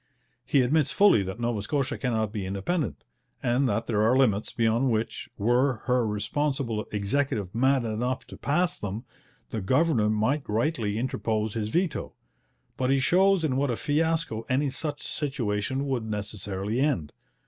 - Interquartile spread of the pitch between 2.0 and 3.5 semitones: No, average, 4.7 semitones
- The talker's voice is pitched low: Yes, low, 120 Hz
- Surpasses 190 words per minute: No, average, 155 wpm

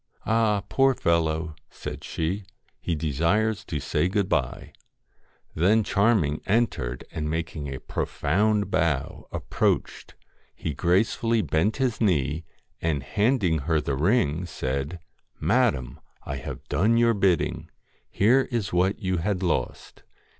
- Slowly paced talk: Yes, slow, 125 wpm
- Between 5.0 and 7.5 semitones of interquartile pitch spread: Yes, wide, 5.5 semitones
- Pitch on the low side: Yes, very low, 90 Hz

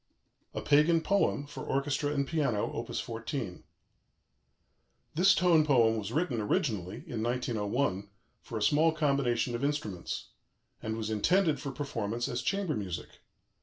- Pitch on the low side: Yes, low, 130 Hz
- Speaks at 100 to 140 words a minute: Yes, slow, 135 wpm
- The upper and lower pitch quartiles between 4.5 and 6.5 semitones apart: Yes, average, 5.3 semitones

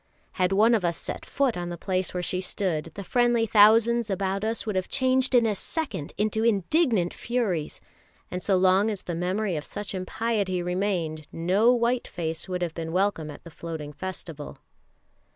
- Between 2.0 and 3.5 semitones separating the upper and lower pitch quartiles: No, average, 4.3 semitones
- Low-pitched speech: No, high, 190 Hz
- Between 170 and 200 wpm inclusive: Yes, average, 185 wpm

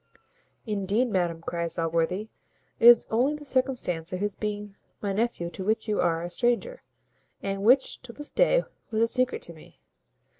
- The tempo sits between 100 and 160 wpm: No, average, 175 wpm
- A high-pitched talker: Yes, high, 210 Hz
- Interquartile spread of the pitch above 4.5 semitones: Yes, wide, 5.5 semitones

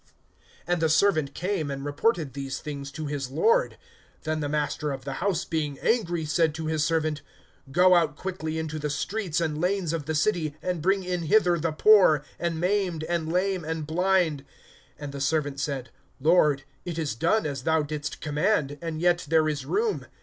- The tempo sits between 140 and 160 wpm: No, average, 185 wpm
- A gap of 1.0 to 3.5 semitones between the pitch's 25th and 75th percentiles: Yes, average, 3.2 semitones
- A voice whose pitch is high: No, medium, 160 Hz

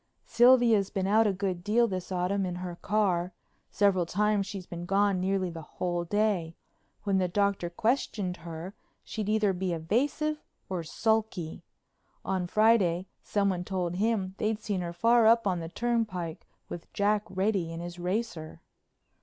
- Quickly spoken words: No, average, 155 wpm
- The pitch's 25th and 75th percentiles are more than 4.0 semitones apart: No, average, 3.3 semitones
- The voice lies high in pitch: Yes, high, 195 Hz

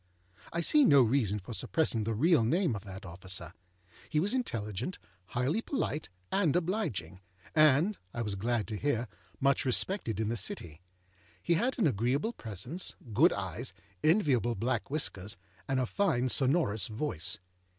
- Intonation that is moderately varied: No, wide, 7.4 semitones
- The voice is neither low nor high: No, low, 125 Hz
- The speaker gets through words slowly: No, average, 150 wpm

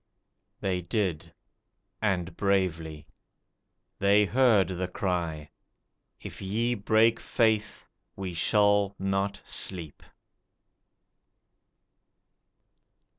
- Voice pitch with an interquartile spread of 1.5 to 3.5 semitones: Yes, average, 2.7 semitones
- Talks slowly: Yes, slow, 75 wpm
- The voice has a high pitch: No, very low, 95 Hz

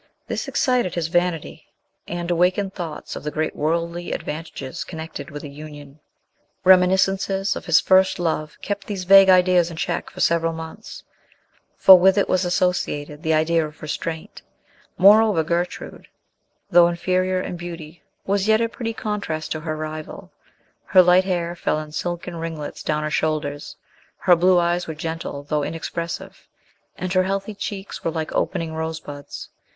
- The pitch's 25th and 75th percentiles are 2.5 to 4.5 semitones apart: Yes, average, 2.8 semitones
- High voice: No, medium, 170 Hz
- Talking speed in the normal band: Yes, average, 155 wpm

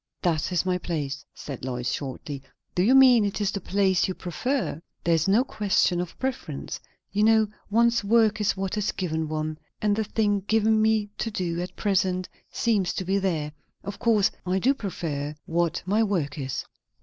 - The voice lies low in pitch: No, high, 190 Hz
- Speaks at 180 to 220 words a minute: Yes, average, 185 wpm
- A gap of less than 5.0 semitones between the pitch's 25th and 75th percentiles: Yes, average, 4.5 semitones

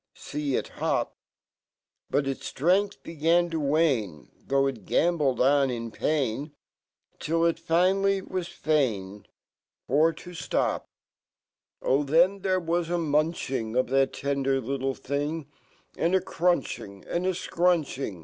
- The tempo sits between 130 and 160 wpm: Yes, slow, 135 wpm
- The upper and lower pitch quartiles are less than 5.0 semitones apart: Yes, average, 4.3 semitones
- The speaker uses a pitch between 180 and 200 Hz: No, medium, 150 Hz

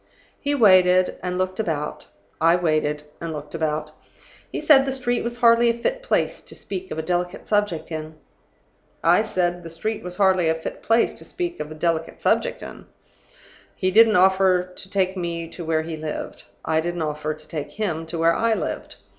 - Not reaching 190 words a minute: No, average, 195 wpm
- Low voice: No, medium, 180 Hz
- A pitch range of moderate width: Yes, average, 4.4 semitones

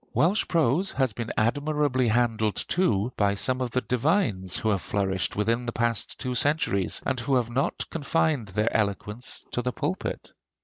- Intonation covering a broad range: No, average, 4.5 semitones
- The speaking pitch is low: Yes, low, 120 Hz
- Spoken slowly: No, average, 170 wpm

